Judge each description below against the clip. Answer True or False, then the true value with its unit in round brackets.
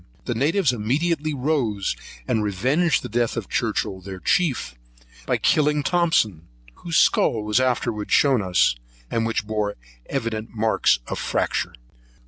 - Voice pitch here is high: False (115 Hz)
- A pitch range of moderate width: False (5.9 semitones)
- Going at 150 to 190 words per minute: False (135 wpm)